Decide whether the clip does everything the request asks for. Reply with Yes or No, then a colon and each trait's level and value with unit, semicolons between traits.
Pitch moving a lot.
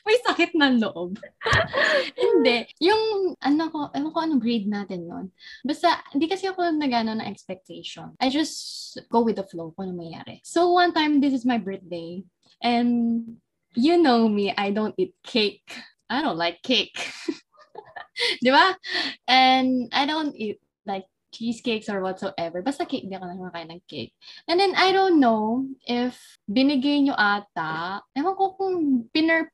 Yes: wide, 8.0 semitones